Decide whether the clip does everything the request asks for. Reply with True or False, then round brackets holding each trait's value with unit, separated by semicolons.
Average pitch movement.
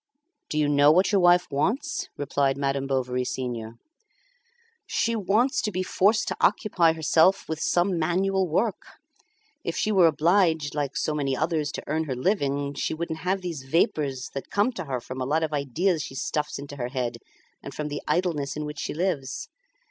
True (4.8 semitones)